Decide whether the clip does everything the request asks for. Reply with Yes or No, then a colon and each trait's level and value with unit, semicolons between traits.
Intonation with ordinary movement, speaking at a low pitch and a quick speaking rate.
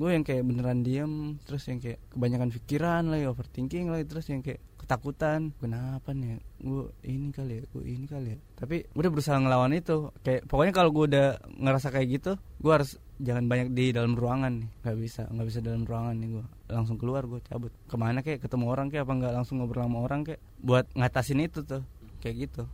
Yes: average, 3.0 semitones; low, 130 Hz; fast, 210 wpm